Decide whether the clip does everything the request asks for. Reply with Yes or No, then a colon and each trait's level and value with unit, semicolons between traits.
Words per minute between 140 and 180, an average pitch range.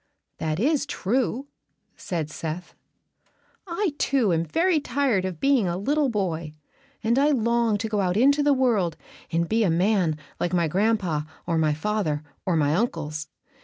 No: average, 165 wpm; wide, 7.3 semitones